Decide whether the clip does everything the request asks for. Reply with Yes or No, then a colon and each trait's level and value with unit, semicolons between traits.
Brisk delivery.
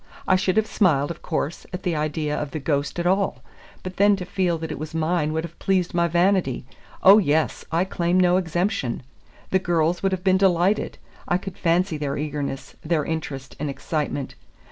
No: average, 195 wpm